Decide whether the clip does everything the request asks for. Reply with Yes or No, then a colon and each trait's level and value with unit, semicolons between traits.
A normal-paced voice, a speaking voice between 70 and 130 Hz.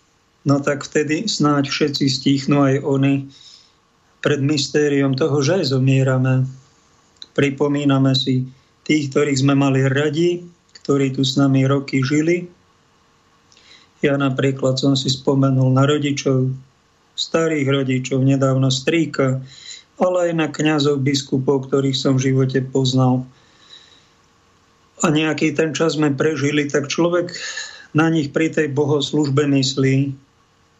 No: average, 120 wpm; medium, 140 Hz